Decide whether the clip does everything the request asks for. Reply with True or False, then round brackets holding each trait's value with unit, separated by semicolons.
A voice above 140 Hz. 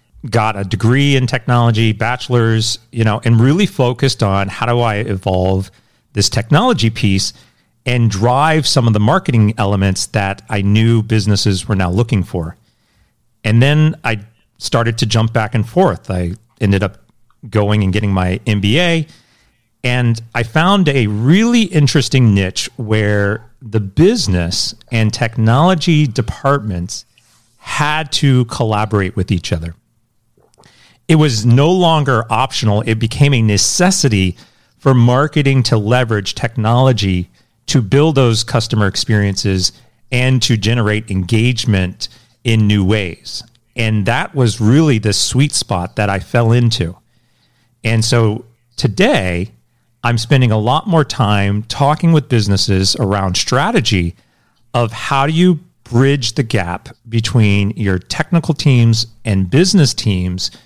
False (115 Hz)